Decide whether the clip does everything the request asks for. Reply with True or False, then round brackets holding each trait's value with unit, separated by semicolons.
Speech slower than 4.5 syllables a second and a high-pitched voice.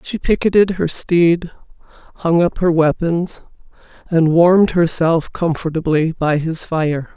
False (4.1 syllables/s; 170 Hz)